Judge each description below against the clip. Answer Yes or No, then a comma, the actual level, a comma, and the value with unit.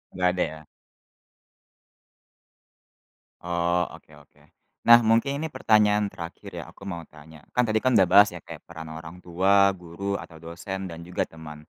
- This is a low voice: Yes, very low, 90 Hz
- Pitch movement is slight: No, average, 3.6 semitones